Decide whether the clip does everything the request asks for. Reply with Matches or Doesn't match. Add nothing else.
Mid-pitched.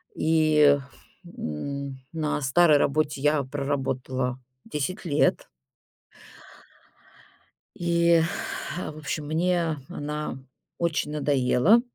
Matches